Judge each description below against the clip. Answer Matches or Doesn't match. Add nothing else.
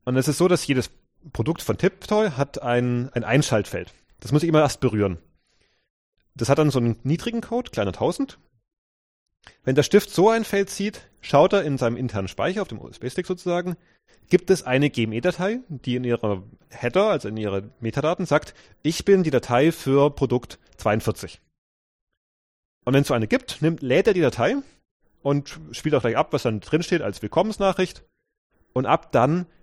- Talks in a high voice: Doesn't match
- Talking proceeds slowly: Doesn't match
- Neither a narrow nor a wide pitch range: Doesn't match